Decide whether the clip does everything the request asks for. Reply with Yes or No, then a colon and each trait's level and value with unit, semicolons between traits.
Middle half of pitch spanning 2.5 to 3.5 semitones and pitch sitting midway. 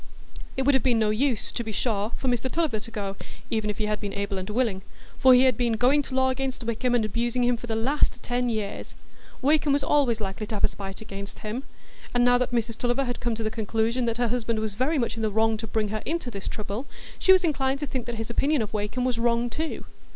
No: average, 3.0 semitones; high, 235 Hz